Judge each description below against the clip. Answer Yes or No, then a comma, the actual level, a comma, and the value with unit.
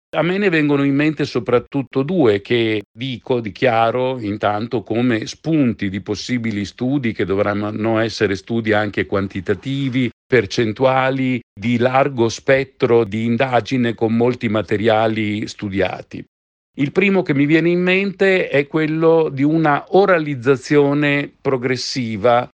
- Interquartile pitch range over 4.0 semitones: Yes, average, 4.4 semitones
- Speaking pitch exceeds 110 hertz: Yes, low, 125 Hz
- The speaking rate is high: No, average, 120 wpm